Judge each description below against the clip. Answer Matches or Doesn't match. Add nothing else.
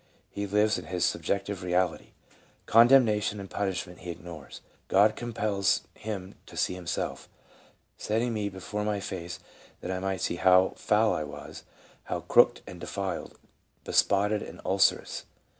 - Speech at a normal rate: Matches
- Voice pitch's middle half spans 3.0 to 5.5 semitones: Doesn't match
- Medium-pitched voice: Doesn't match